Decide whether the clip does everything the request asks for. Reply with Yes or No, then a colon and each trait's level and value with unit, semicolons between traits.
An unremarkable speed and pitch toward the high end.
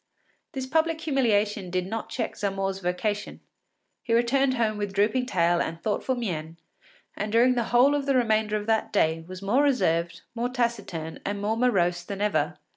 Yes: average, 175 wpm; high, 210 Hz